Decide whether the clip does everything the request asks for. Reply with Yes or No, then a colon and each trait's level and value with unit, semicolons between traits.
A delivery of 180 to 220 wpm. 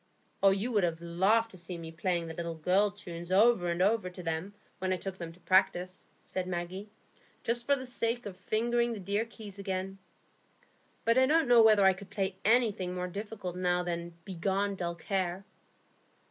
Yes: average, 190 wpm